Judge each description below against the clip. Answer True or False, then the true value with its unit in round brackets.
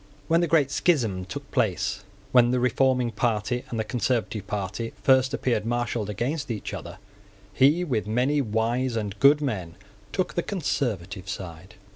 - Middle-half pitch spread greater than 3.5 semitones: True (4.3 semitones)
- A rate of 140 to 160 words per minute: True (155 wpm)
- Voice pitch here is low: True (120 Hz)